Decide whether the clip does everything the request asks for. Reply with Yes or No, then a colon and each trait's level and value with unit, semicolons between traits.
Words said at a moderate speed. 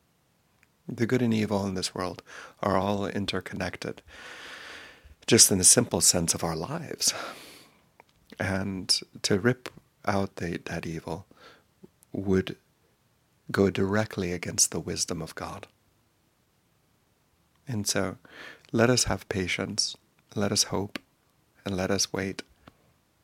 No: slow, 120 wpm